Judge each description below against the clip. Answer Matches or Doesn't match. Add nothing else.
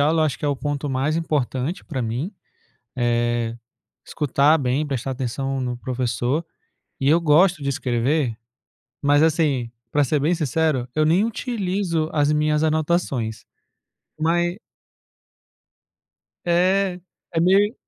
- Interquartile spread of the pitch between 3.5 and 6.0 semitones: Matches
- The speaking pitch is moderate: Matches